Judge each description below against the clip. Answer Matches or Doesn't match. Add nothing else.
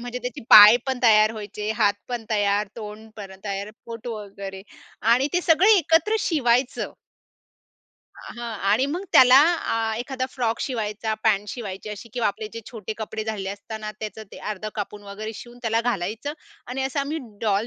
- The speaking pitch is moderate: Doesn't match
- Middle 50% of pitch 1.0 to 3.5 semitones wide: Matches